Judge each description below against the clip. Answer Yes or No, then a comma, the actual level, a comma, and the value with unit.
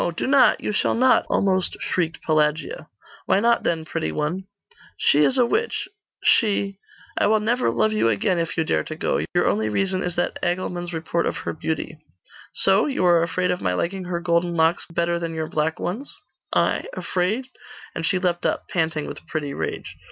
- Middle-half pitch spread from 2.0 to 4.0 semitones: Yes, average, 3.3 semitones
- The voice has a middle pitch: Yes, medium, 175 Hz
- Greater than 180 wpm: Yes, average, 190 wpm